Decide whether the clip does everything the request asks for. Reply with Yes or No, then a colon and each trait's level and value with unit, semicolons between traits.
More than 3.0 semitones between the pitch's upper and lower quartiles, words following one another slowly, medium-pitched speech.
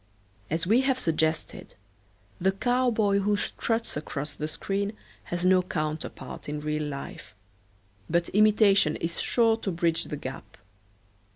Yes: average, 5.3 semitones; slow, 130 wpm; medium, 180 Hz